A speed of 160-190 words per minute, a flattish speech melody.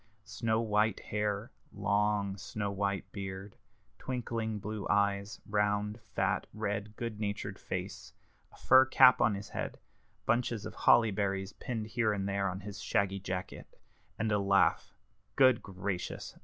No: average, 140 wpm; narrow, 1.7 semitones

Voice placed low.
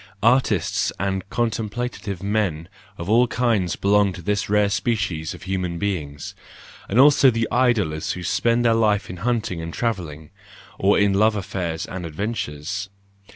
Yes: low, 100 Hz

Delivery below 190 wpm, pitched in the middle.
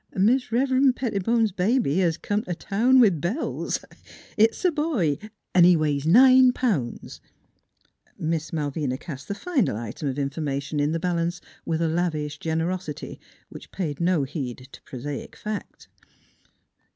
Yes: average, 150 wpm; medium, 170 Hz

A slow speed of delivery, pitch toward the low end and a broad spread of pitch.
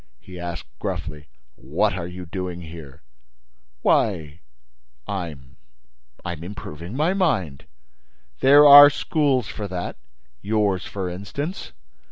Yes: slow, 100 wpm; very low, 90 Hz; wide, 6.3 semitones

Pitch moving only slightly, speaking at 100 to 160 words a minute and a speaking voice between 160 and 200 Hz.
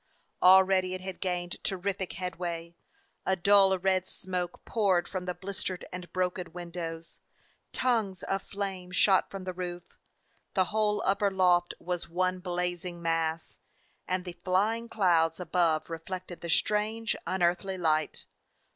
Yes: narrow, 1.6 semitones; average, 140 wpm; medium, 185 Hz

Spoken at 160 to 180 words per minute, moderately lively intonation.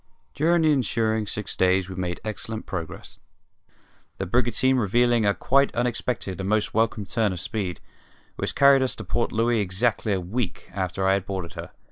Yes: average, 175 wpm; average, 4.2 semitones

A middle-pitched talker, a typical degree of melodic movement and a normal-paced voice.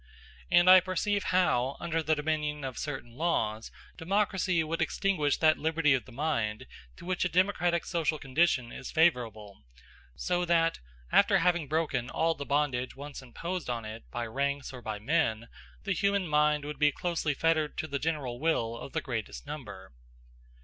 Yes: medium, 150 Hz; average, 5.0 semitones; average, 170 wpm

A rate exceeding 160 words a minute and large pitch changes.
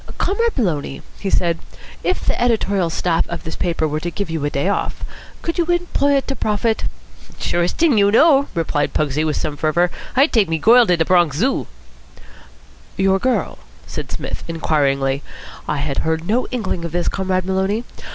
Yes: average, 180 wpm; wide, 6.5 semitones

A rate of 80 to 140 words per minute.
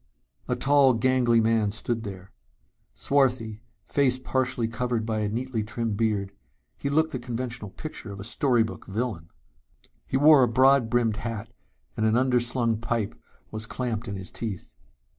No: average, 160 wpm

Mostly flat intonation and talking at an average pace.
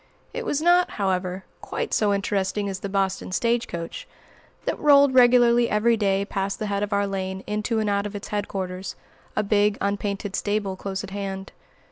Yes: narrow, 2.0 semitones; average, 180 wpm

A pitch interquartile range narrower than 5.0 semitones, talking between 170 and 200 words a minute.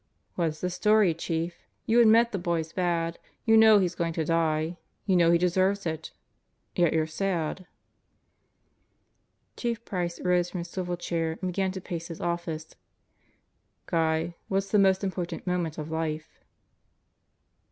No: narrow, 2.6 semitones; average, 150 wpm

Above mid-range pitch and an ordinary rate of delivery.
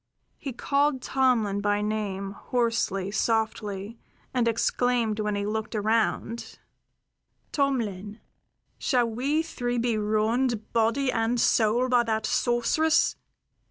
No: high, 230 Hz; slow, 110 wpm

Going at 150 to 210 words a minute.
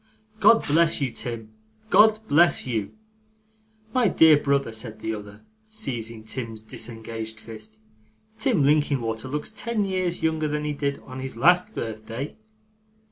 No: slow, 135 wpm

